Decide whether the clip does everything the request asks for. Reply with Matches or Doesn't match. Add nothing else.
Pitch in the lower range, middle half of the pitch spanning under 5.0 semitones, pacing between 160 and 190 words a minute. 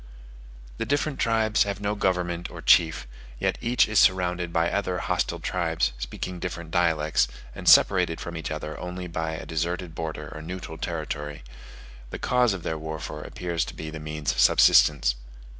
Matches